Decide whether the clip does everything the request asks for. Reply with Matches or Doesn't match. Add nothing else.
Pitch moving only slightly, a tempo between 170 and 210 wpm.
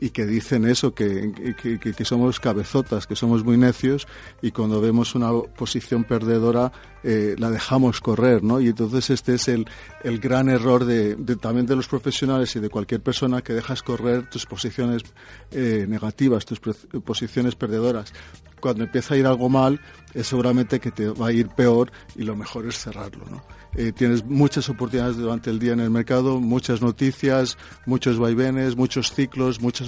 Matches